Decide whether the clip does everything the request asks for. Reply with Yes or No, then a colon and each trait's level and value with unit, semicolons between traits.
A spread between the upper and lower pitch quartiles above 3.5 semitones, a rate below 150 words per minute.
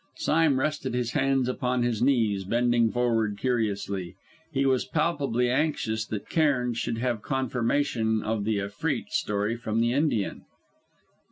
No: average, 3.2 semitones; average, 140 wpm